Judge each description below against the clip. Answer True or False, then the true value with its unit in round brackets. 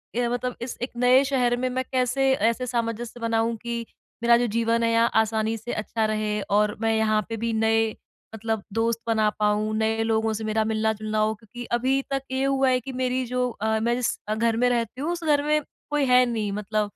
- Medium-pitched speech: False (230 Hz)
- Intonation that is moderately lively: False (2.3 semitones)